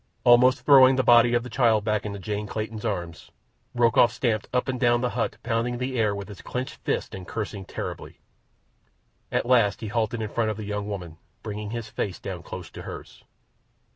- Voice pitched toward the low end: Yes, low, 110 Hz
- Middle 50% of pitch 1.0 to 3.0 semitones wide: Yes, average, 2.7 semitones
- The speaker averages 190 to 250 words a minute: Yes, average, 200 wpm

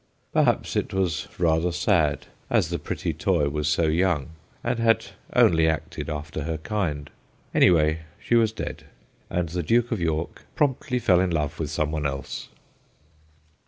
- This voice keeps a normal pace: Yes, average, 160 wpm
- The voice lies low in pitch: Yes, very low, 85 Hz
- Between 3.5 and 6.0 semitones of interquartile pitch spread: Yes, average, 3.9 semitones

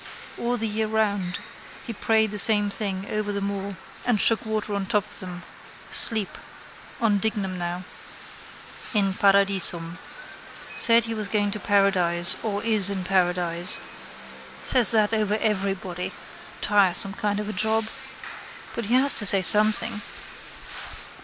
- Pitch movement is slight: Yes, narrow, 2.2 semitones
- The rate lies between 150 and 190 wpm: No, average, 140 wpm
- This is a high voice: Yes, high, 205 Hz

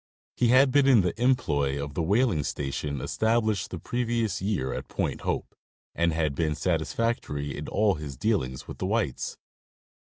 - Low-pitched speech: Yes, very low, 90 Hz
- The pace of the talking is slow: No, average, 170 wpm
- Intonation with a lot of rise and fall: Yes, wide, 8.0 semitones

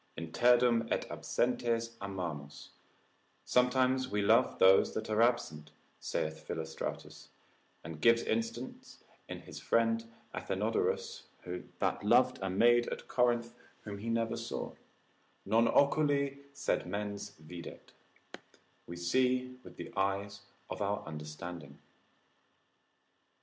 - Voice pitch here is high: No, low, 115 Hz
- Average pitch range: Yes, average, 4.8 semitones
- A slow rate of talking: Yes, slow, 110 wpm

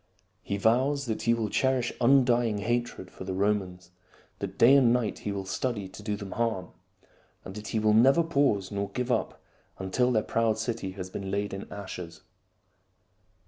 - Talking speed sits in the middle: Yes, average, 180 wpm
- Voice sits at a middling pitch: No, low, 110 Hz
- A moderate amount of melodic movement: Yes, average, 3.6 semitones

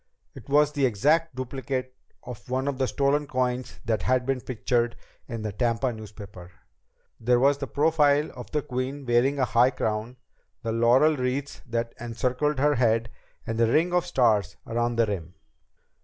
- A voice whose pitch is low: Yes, low, 125 Hz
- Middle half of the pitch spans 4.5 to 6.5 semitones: No, average, 3.2 semitones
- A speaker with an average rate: Yes, average, 170 wpm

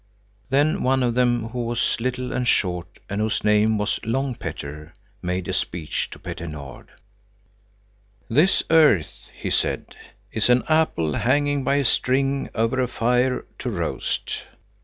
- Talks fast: No, average, 150 wpm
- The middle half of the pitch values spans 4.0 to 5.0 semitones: Yes, average, 4.3 semitones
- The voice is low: Yes, low, 120 Hz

